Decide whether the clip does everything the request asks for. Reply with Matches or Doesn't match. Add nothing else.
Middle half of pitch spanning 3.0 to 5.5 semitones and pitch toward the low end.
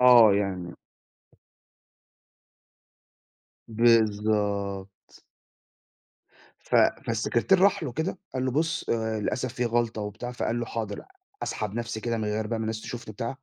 Doesn't match